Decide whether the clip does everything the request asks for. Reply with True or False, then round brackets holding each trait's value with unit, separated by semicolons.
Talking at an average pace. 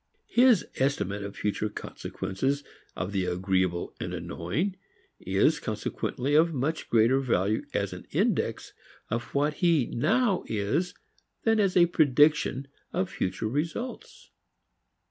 False (125 wpm)